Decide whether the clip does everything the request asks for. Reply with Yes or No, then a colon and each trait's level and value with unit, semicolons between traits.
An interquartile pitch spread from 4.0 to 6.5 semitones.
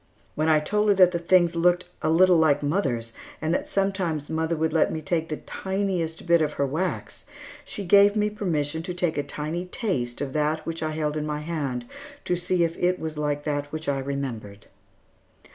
No: average, 3.3 semitones